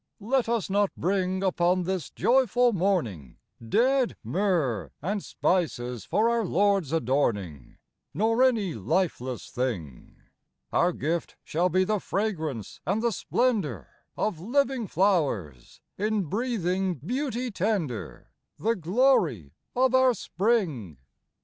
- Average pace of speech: No, slow, 115 wpm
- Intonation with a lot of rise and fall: Yes, wide, 7.4 semitones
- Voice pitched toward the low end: No, medium, 185 Hz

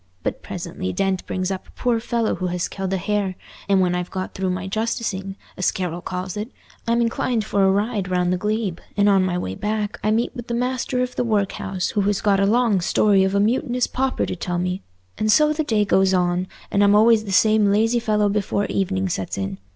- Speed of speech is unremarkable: No, fast, 230 wpm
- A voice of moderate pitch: No, high, 200 Hz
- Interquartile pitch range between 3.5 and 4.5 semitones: No, average, 3.0 semitones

